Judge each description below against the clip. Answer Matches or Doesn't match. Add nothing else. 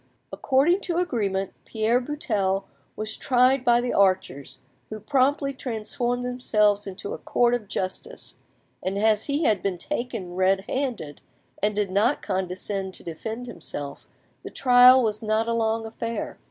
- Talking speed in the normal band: Matches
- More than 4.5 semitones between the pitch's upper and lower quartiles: Doesn't match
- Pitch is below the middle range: Doesn't match